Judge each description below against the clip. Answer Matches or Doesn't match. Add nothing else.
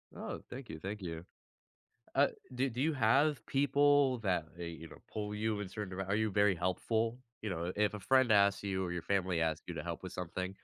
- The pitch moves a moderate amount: Matches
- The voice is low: Matches